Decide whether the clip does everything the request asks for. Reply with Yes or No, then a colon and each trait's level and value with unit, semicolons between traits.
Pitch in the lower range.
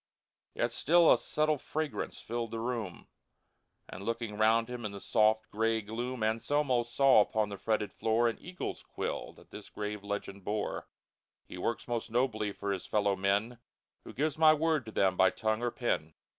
Yes: low, 115 Hz